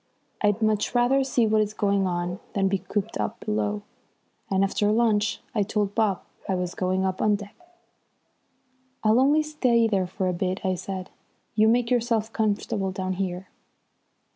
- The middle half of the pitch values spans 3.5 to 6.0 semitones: No, average, 2.9 semitones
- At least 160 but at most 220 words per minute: Yes, average, 165 wpm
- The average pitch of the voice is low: No, high, 205 Hz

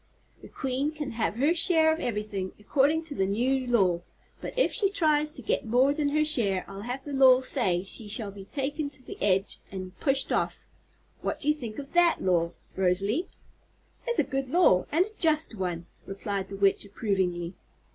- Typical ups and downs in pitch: No, wide, 7.2 semitones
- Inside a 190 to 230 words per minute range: Yes, average, 195 wpm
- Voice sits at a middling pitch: No, very high, 250 Hz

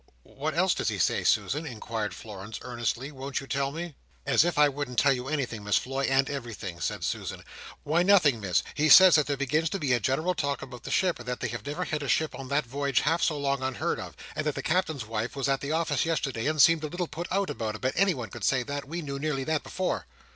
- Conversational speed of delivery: No, fast, 255 wpm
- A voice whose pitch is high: No, medium, 140 Hz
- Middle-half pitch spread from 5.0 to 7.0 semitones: No, average, 3.9 semitones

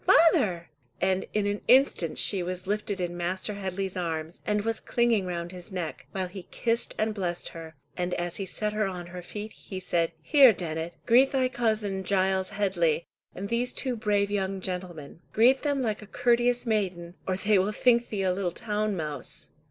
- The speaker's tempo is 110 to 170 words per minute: No, average, 190 wpm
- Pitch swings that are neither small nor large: Yes, average, 3.4 semitones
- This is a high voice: Yes, high, 195 Hz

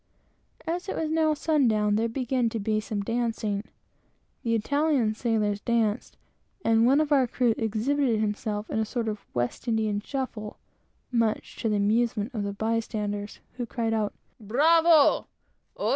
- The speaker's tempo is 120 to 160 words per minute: Yes, average, 150 wpm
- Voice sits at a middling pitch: No, high, 225 Hz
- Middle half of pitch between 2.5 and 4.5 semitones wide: Yes, average, 3.4 semitones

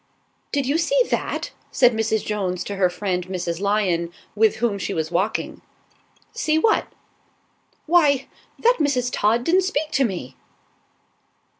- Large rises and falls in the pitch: Yes, wide, 7.6 semitones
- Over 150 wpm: No, average, 140 wpm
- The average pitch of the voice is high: Yes, high, 220 Hz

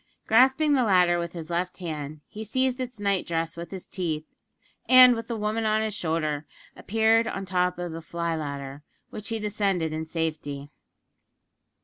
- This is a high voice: No, medium, 180 Hz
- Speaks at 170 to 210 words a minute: Yes, average, 175 wpm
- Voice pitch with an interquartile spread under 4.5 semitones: No, average, 5.3 semitones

